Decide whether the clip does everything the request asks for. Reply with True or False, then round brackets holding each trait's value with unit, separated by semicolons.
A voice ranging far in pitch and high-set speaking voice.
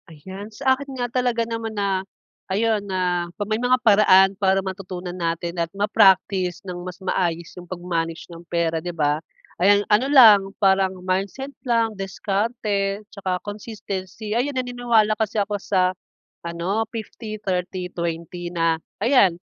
False (3.4 semitones; 195 Hz)